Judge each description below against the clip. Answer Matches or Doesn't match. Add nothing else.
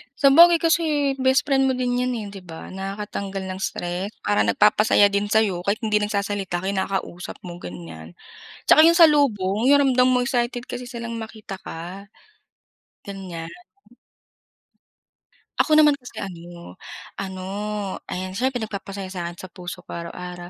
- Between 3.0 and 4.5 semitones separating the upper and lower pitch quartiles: Doesn't match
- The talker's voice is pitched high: Matches